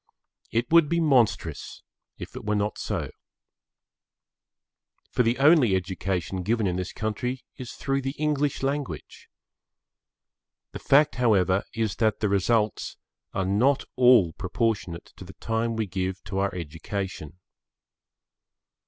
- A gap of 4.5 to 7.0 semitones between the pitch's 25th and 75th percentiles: Yes, average, 5.1 semitones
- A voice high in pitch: No, low, 110 Hz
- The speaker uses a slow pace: Yes, slow, 130 wpm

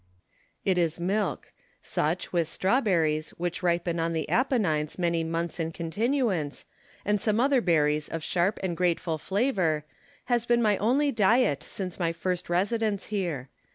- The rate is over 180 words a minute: No, average, 150 wpm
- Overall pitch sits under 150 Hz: No, medium, 180 Hz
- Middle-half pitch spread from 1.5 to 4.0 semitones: No, average, 4.5 semitones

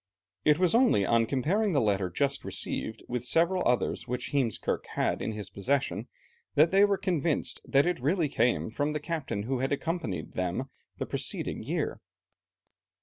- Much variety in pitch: Yes, wide, 6.3 semitones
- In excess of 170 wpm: No, average, 165 wpm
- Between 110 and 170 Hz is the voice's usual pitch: Yes, medium, 140 Hz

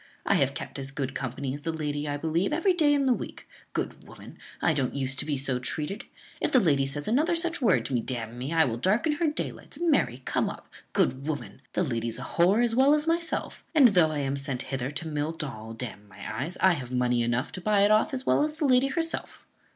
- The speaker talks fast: Yes, fast, 250 wpm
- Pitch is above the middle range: No, medium, 150 Hz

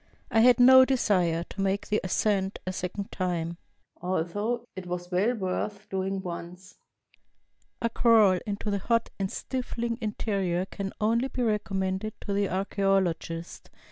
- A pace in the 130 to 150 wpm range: Yes, average, 140 wpm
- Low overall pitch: No, high, 195 Hz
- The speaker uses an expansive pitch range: No, average, 3.1 semitones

